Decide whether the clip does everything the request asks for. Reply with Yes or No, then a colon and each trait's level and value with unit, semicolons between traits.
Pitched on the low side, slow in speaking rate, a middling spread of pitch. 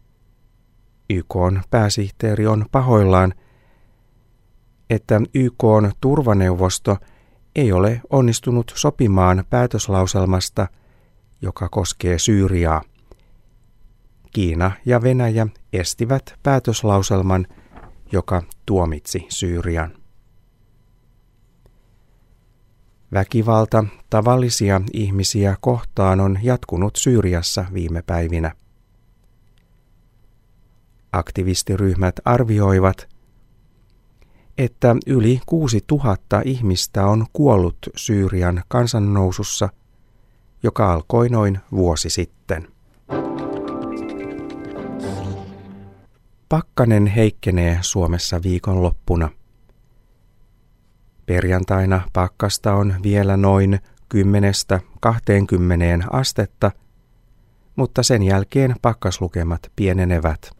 Yes: low, 100 Hz; slow, 65 wpm; average, 3.7 semitones